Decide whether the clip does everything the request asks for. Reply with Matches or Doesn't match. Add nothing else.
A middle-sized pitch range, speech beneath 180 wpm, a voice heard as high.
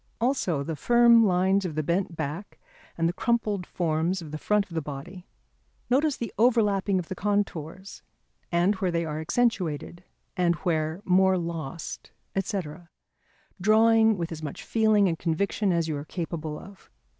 Doesn't match